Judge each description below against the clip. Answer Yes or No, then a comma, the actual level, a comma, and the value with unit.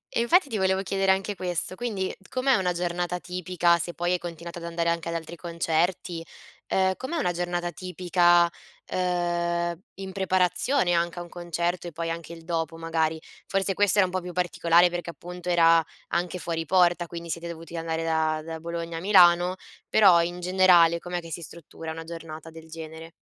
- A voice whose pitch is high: No, medium, 175 Hz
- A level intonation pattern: Yes, narrow, 1.5 semitones